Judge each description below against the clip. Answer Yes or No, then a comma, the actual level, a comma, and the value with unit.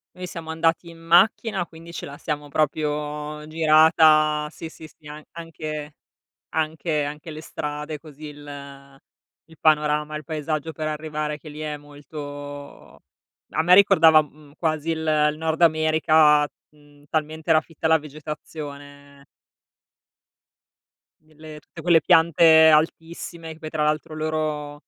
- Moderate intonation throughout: No, narrow, 1.3 semitones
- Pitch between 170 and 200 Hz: No, medium, 155 Hz